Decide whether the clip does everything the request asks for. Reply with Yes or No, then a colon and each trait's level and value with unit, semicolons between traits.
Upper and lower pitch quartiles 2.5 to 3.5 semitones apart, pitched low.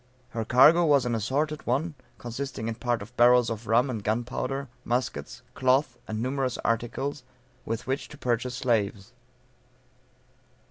Yes: average, 2.8 semitones; low, 125 Hz